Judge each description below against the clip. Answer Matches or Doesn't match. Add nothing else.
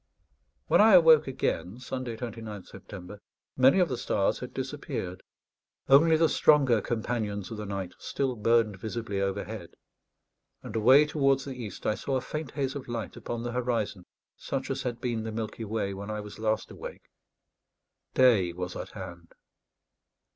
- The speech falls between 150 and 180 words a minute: Matches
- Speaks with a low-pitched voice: Matches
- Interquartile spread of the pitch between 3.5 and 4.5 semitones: Matches